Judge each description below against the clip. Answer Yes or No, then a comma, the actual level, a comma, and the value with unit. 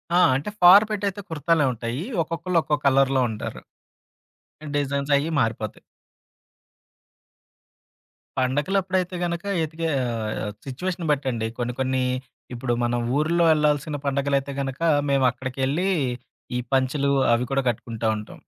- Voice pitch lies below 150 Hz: Yes, medium, 140 Hz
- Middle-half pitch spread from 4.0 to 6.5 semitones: Yes, average, 4.6 semitones